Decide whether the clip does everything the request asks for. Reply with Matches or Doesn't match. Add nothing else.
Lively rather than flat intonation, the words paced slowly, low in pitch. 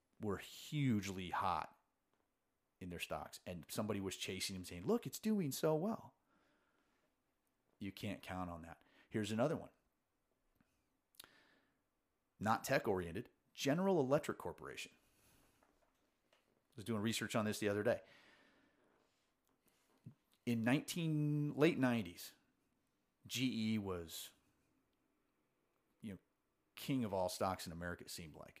Matches